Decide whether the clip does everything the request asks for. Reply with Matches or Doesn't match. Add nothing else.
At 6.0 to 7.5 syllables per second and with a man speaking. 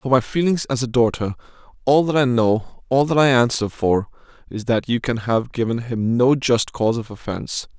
Doesn't match